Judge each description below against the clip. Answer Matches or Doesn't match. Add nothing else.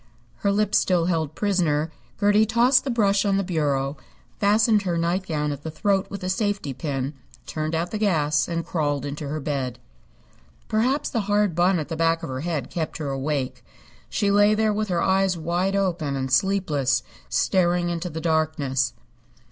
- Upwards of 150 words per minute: Matches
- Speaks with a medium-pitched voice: Matches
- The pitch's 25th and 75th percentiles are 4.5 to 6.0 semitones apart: Matches